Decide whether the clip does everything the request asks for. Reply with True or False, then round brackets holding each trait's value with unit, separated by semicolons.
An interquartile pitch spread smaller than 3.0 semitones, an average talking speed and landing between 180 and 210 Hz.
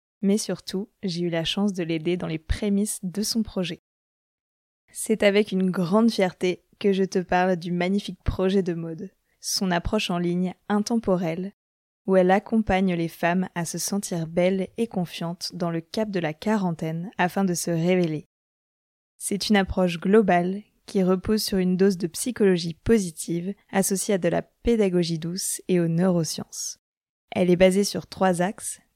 True (2.6 semitones; 170 wpm; 185 Hz)